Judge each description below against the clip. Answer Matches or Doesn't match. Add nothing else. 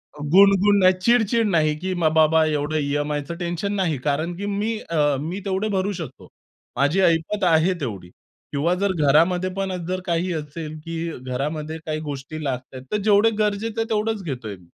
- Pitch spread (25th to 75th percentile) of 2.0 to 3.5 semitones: Doesn't match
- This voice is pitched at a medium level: Matches